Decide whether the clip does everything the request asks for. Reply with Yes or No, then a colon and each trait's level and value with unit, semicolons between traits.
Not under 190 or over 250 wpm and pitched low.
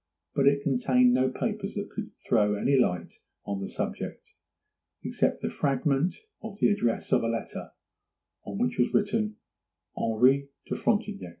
No: average, 145 wpm; low, 130 Hz